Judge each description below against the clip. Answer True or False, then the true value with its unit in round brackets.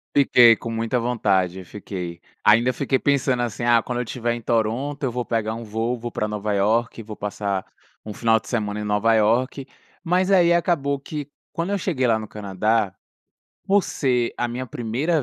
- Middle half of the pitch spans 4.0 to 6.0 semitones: False (3.6 semitones)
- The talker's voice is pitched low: True (115 Hz)